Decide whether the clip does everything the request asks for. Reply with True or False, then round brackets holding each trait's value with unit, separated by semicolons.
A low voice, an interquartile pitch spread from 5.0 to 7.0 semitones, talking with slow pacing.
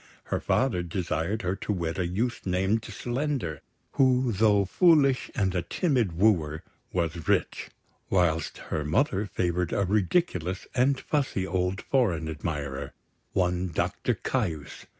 True (95 Hz; 5.5 semitones; 130 wpm)